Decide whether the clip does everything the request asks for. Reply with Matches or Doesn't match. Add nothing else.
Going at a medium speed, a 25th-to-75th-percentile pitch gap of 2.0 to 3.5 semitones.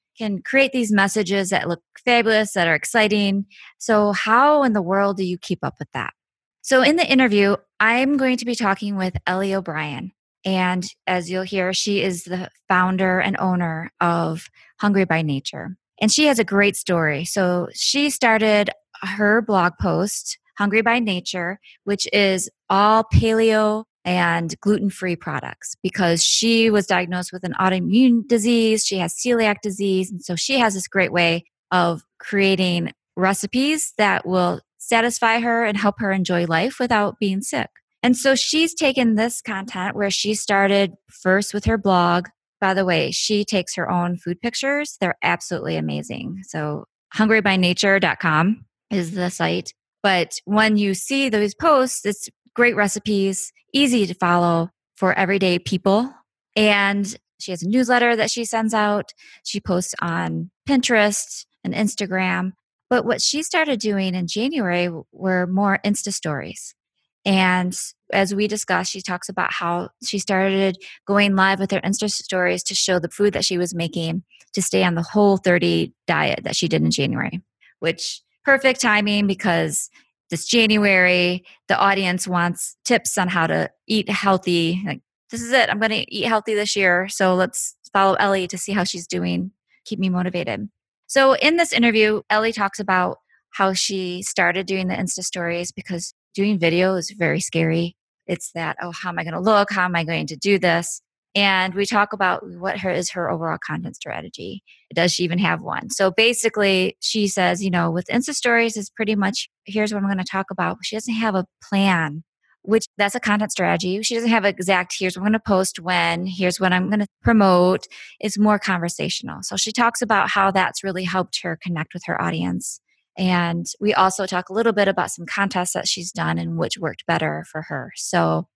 Matches